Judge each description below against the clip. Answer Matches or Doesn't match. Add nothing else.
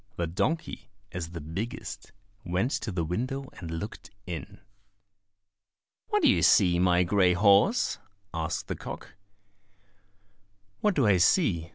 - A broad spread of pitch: Matches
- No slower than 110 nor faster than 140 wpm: Matches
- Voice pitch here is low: Matches